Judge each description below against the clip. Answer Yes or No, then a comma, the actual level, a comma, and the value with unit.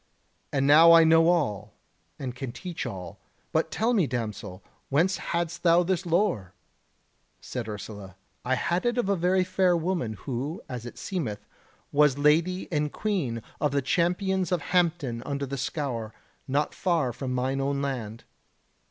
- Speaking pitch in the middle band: Yes, medium, 145 Hz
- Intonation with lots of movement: Yes, wide, 6.1 semitones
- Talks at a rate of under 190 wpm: Yes, average, 160 wpm